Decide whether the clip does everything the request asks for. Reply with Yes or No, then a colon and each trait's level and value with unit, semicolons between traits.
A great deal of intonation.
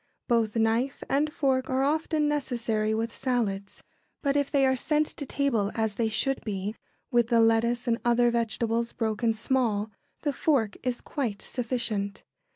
No: average, 3.2 semitones